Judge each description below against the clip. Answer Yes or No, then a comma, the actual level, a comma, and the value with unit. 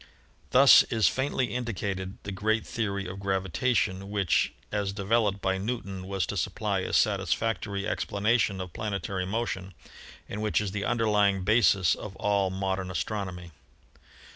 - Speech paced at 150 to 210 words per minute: No, average, 140 wpm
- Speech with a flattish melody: Yes, narrow, 2.2 semitones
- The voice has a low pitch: Yes, low, 100 Hz